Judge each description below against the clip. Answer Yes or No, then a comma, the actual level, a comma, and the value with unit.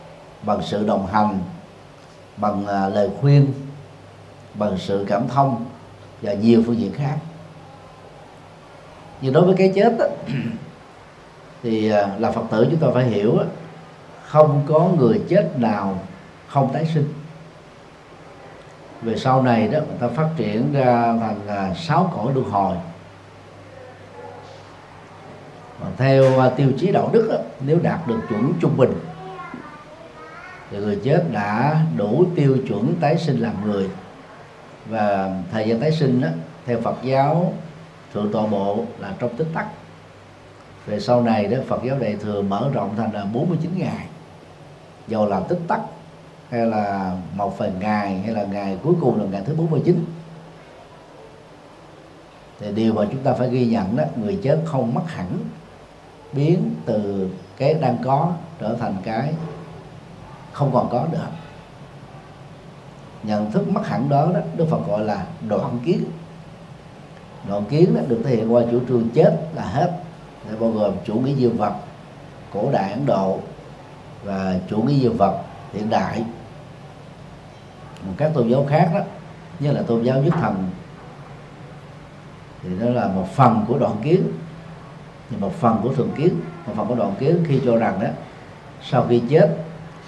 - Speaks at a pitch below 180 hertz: Yes, low, 135 Hz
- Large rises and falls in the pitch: Yes, wide, 6.3 semitones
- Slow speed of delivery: Yes, slow, 155 wpm